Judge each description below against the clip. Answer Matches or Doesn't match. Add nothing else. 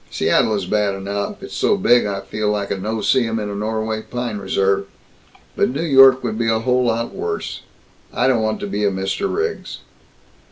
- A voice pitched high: Doesn't match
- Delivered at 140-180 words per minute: Doesn't match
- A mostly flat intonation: Doesn't match